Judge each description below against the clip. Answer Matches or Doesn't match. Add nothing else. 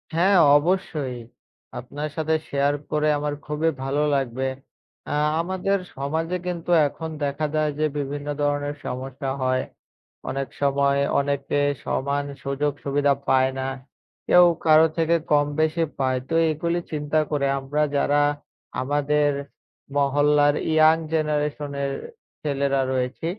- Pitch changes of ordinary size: Doesn't match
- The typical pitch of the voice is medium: Matches